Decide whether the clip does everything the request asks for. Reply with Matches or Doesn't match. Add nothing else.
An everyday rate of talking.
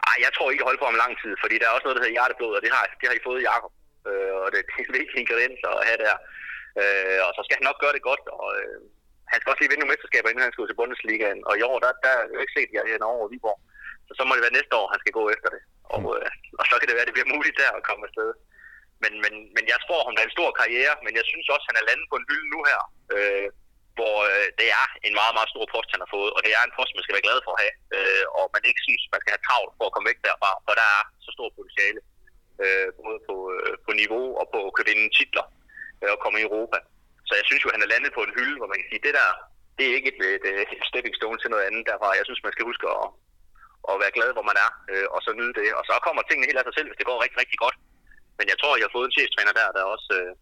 Doesn't match